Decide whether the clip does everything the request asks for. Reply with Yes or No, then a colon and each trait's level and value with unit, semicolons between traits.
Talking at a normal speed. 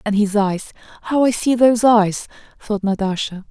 Yes: average, 155 wpm